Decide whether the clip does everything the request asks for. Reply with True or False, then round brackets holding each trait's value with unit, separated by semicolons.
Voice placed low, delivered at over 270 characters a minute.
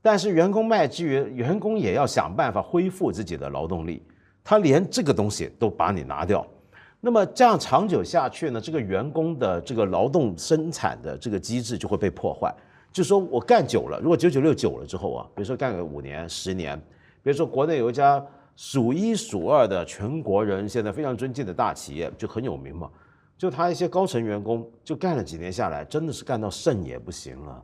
True (130 Hz; 315 characters per minute)